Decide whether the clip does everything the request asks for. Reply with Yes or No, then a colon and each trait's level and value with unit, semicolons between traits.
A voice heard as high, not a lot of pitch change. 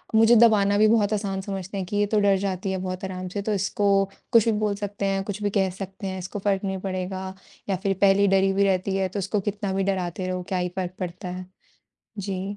Yes: high, 195 Hz; narrow, 1.4 semitones